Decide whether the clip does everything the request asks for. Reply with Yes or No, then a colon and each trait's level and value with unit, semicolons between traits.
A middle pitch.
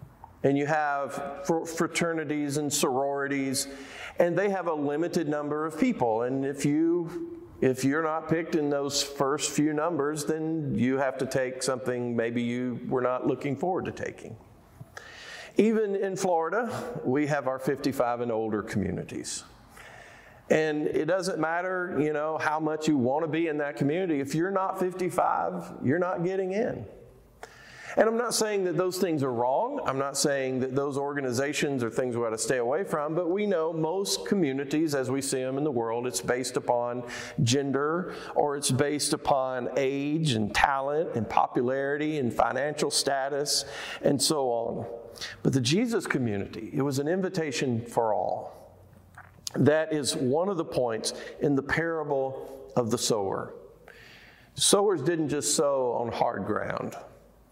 Yes: medium, 145 Hz